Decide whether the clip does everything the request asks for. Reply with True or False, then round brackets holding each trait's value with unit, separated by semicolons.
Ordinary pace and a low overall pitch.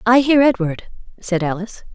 False (155 wpm; 210 Hz)